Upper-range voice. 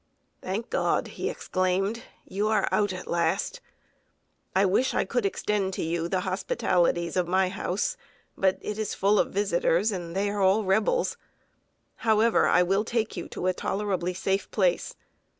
Yes: high, 195 Hz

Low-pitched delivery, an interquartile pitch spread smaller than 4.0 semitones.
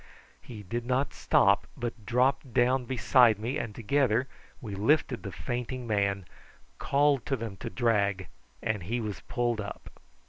Yes: low, 120 Hz; average, 3.5 semitones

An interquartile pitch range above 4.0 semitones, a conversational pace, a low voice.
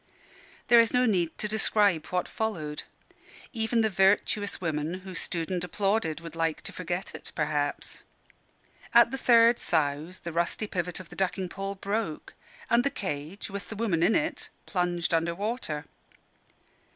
No: average, 4.7 semitones; average, 160 wpm; medium, 185 Hz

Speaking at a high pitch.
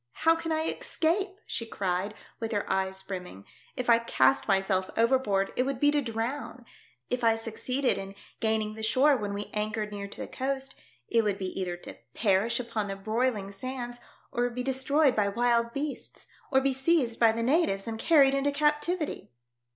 Yes: high, 235 Hz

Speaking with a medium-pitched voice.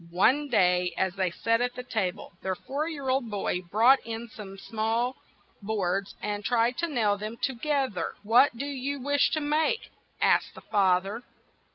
No: high, 230 Hz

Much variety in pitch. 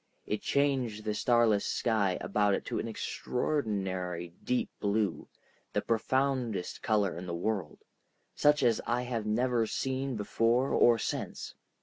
No: average, 3.6 semitones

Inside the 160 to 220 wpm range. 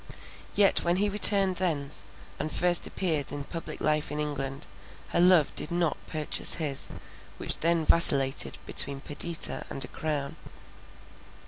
No: average, 140 wpm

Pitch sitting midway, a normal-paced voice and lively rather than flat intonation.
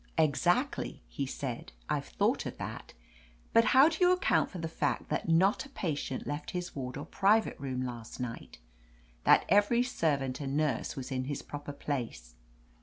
Yes: medium, 145 Hz; average, 175 wpm; wide, 6.9 semitones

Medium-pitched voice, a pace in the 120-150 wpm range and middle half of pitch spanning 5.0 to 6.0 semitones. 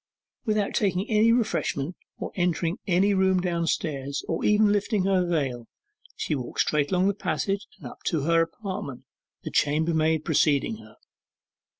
No: medium, 180 Hz; average, 145 wpm; average, 4.4 semitones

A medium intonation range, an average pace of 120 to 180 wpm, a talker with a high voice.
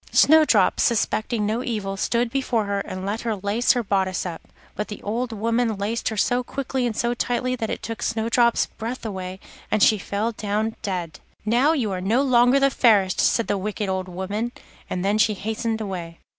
No: average, 3.2 semitones; average, 195 wpm; high, 220 Hz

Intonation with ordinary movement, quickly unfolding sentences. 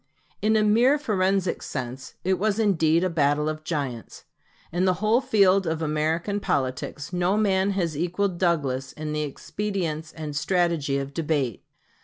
No: average, 4.7 semitones; average, 155 wpm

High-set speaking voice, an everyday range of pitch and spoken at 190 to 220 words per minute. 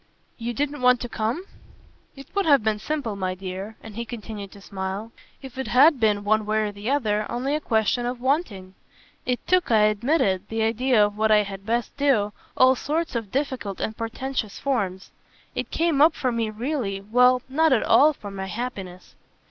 Yes: high, 230 Hz; average, 4.3 semitones; average, 195 wpm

